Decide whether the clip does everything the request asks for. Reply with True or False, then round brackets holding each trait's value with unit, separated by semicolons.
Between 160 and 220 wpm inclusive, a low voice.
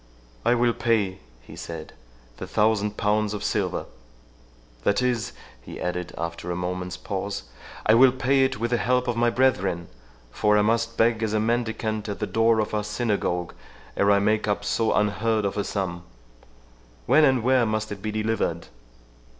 True (170 wpm; 105 Hz)